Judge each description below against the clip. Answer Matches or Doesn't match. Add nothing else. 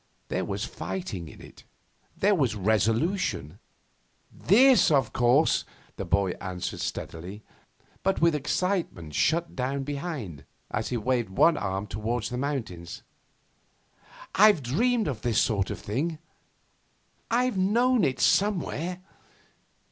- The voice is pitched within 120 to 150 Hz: Matches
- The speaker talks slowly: Matches